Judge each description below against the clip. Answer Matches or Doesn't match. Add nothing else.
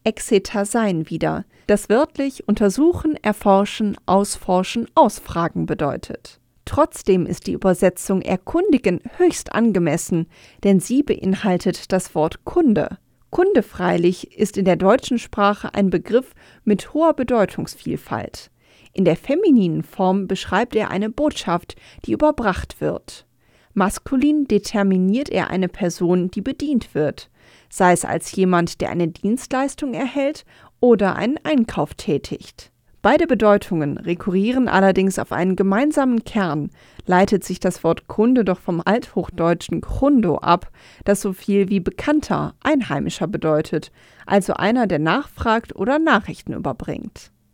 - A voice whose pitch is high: Matches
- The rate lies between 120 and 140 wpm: Matches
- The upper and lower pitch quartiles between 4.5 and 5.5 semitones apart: Matches